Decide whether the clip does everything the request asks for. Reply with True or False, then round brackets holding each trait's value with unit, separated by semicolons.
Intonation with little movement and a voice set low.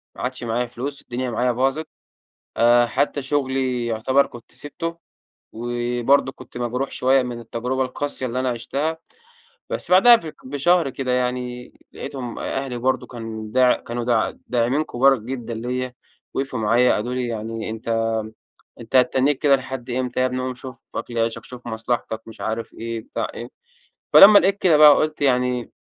True (2.1 semitones; 125 Hz)